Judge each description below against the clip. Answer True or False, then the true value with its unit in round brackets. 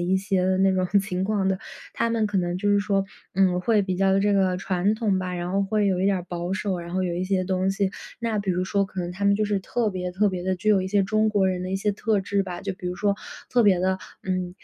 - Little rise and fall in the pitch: True (1.8 semitones)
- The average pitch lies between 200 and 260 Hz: False (190 Hz)